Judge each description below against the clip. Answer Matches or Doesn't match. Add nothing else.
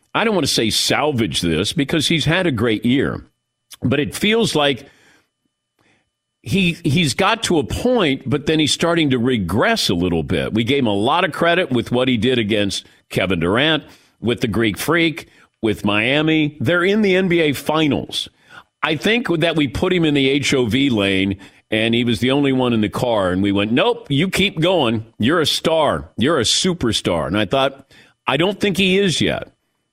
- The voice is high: Doesn't match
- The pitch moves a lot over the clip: Matches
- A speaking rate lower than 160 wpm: Doesn't match